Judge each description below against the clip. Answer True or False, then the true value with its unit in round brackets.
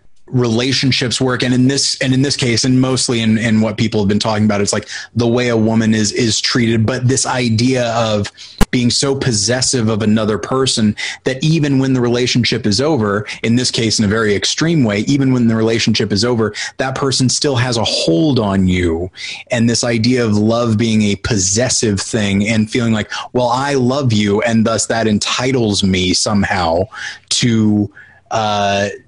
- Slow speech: False (190 wpm)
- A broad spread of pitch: False (3.1 semitones)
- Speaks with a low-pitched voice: True (115 Hz)